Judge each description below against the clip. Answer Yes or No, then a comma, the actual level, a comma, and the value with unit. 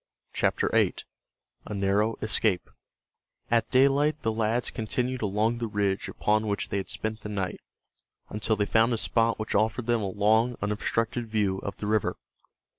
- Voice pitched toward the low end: Yes, low, 110 Hz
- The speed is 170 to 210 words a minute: No, average, 160 wpm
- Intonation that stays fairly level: Yes, narrow, 1.9 semitones